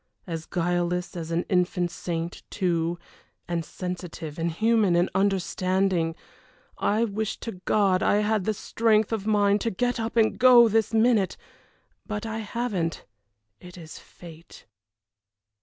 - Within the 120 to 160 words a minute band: Yes, average, 140 wpm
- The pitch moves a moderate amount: Yes, average, 4.0 semitones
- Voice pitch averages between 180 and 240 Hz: Yes, high, 190 Hz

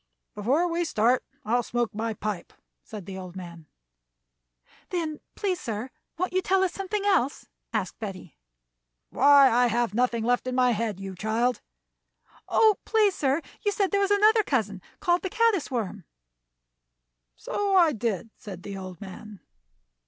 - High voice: Yes, high, 245 Hz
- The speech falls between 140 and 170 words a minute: Yes, average, 160 wpm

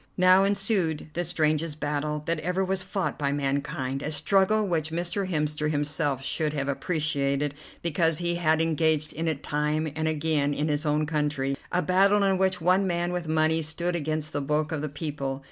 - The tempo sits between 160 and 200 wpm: Yes, average, 185 wpm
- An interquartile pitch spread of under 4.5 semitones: Yes, average, 2.9 semitones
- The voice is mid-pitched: Yes, medium, 155 Hz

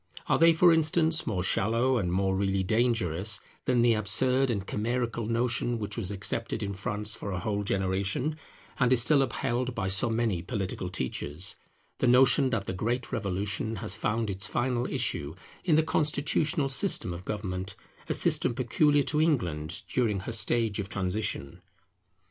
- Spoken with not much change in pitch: No, average, 4.6 semitones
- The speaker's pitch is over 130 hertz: No, low, 110 Hz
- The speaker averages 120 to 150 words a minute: No, average, 165 wpm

